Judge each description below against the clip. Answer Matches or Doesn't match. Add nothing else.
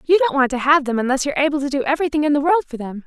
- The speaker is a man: Doesn't match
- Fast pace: Matches